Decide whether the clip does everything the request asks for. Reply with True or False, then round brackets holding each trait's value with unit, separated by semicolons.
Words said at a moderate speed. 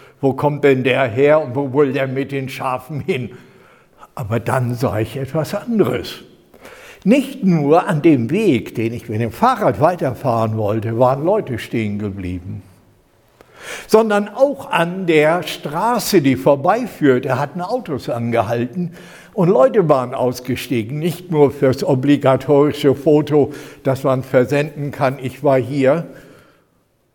True (135 wpm)